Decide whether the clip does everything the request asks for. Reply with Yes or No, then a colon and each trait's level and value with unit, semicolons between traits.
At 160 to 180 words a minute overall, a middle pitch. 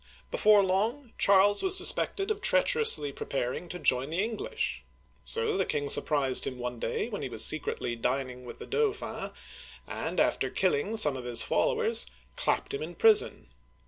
Yes: average, 165 wpm; medium, 180 Hz